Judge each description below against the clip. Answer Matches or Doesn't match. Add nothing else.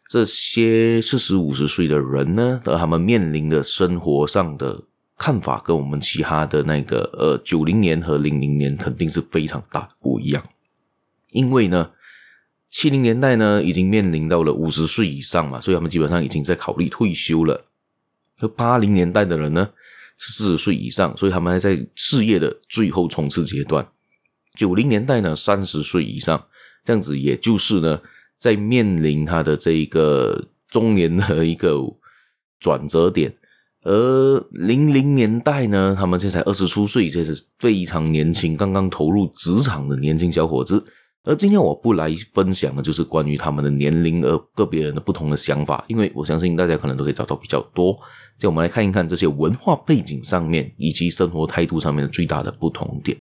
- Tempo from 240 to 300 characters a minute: Matches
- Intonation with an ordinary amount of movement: Matches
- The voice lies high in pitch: Doesn't match